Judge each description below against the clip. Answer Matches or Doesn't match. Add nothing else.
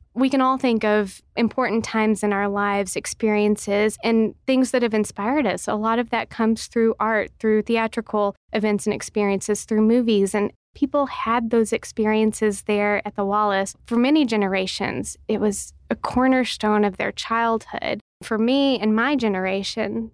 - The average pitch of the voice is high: Matches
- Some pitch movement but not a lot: Doesn't match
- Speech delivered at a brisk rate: Doesn't match